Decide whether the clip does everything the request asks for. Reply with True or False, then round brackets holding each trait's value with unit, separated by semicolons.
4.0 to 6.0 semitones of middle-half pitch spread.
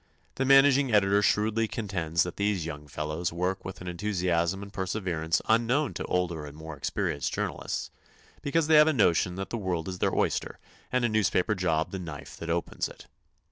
True (4.6 semitones)